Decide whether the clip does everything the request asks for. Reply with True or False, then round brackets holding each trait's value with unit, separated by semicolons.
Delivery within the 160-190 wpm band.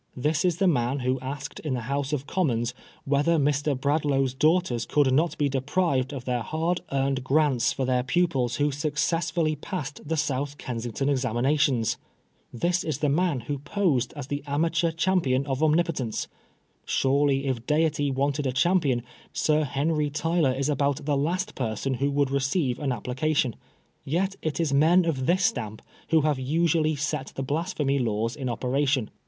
True (170 wpm)